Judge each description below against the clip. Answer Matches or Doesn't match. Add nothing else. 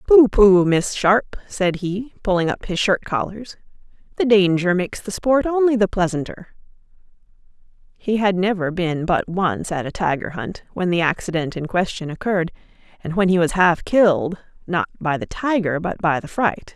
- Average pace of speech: Matches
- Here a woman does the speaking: Matches